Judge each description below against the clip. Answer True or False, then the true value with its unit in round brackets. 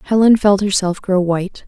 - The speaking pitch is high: True (195 Hz)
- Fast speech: False (180 wpm)